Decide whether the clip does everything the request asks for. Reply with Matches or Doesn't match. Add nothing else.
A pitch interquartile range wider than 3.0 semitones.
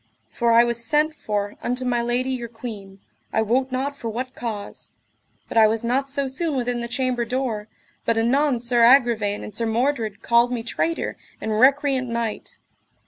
Doesn't match